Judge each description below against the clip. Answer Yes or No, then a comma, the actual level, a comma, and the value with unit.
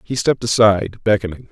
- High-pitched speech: No, low, 105 Hz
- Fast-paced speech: No, average, 160 wpm